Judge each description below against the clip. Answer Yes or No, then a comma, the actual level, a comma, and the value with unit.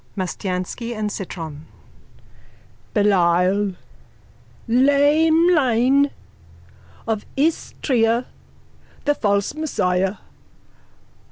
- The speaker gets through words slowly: Yes, slow, 60 wpm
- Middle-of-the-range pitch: No, high, 225 Hz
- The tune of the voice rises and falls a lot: Yes, wide, 6.7 semitones